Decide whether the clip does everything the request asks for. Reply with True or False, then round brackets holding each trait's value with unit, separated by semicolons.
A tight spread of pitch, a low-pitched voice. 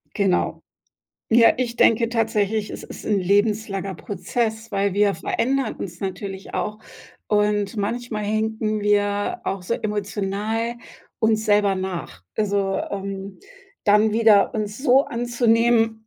False (2.1 semitones; 210 Hz)